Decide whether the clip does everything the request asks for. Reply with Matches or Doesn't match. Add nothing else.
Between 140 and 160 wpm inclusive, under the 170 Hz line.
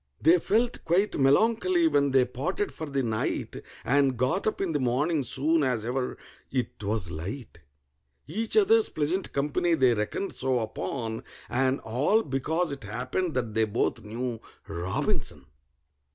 Matches